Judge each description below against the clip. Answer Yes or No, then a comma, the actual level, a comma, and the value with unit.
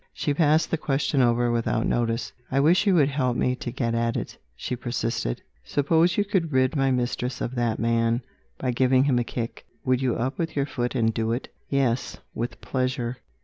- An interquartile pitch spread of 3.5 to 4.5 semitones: No, average, 2.9 semitones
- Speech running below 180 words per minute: No, average, 200 wpm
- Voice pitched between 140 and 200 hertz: No, low, 125 Hz